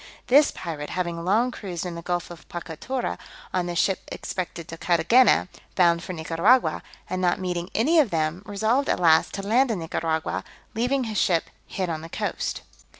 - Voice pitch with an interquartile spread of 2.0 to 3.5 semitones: No, average, 4.6 semitones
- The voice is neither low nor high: Yes, medium, 180 Hz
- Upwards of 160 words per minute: Yes, average, 180 wpm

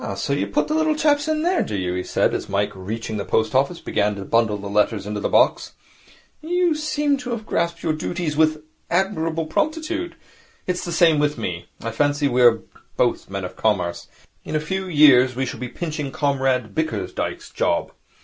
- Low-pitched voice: No, medium, 145 Hz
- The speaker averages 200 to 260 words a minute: Yes, fast, 205 wpm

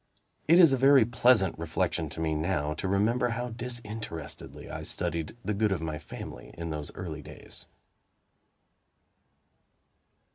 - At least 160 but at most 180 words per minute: No, average, 140 wpm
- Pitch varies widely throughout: Yes, wide, 6.8 semitones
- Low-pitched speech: Yes, low, 100 Hz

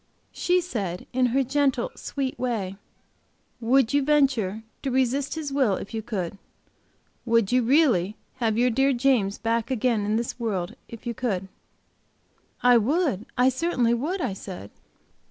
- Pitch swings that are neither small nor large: Yes, average, 4.0 semitones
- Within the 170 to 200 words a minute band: No, average, 155 wpm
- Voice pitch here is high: Yes, high, 240 Hz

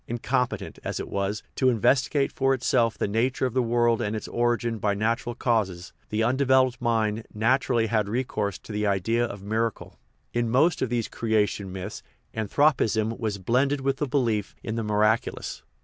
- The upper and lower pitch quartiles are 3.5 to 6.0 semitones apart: No, average, 3.0 semitones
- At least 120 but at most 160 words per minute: No, average, 175 wpm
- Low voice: Yes, low, 115 Hz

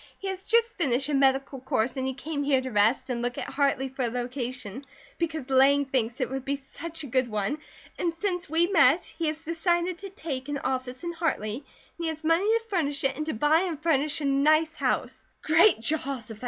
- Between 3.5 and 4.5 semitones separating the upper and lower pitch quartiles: Yes, average, 4.1 semitones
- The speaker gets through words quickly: Yes, fast, 220 wpm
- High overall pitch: Yes, very high, 285 Hz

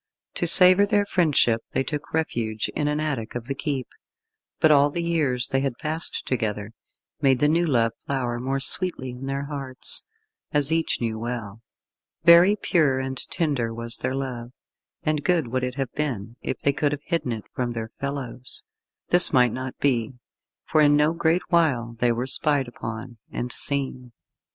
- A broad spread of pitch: No, average, 4.0 semitones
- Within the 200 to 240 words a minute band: No, average, 175 wpm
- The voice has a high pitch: No, low, 135 Hz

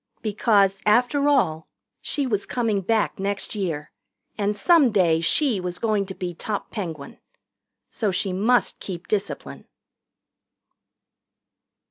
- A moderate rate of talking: No, slow, 120 wpm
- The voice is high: Yes, high, 205 Hz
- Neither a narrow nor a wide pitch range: Yes, average, 3.7 semitones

